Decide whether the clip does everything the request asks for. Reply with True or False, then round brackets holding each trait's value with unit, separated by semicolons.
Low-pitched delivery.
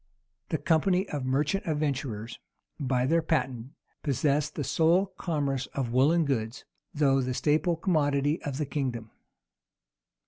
False (145 Hz)